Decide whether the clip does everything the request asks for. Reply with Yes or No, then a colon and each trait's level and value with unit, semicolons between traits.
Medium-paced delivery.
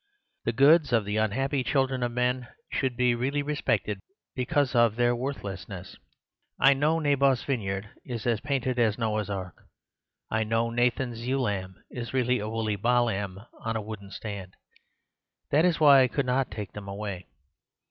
Yes: average, 170 wpm